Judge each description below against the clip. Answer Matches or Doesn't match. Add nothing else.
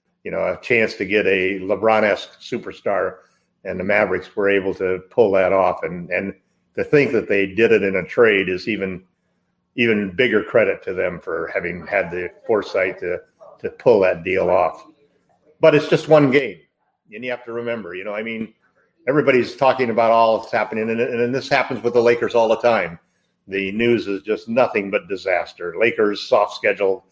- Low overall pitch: Matches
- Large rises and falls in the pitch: Matches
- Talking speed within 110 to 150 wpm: Doesn't match